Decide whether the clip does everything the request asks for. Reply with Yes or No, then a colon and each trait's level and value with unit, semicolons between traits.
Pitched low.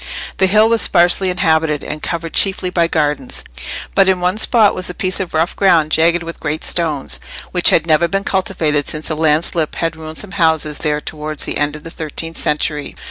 No: medium, 165 Hz